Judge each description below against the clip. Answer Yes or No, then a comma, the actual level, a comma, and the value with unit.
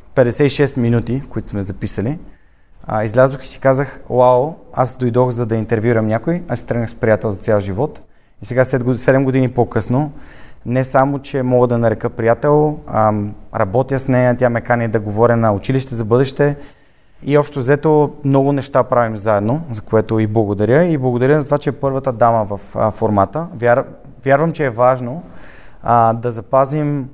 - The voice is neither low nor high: No, low, 125 Hz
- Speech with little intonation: No, average, 3.2 semitones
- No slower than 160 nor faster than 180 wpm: Yes, fast, 165 wpm